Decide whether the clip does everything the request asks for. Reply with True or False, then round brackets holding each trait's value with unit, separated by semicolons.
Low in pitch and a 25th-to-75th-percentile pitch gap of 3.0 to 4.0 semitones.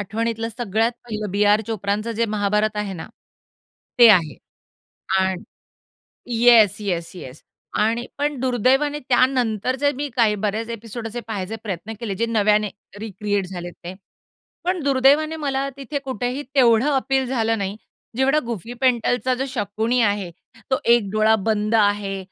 False (225 Hz; 3.7 semitones)